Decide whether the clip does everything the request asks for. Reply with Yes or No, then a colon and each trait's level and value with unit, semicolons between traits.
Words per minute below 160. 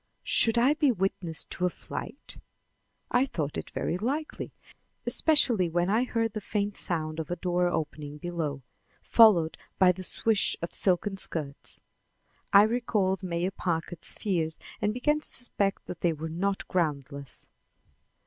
Yes: average, 150 wpm